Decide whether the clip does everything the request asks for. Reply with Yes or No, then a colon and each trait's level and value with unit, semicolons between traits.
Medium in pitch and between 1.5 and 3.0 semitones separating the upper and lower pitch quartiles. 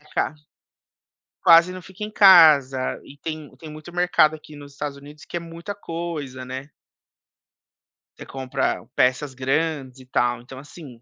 No: medium, 150 Hz; average, 4.0 semitones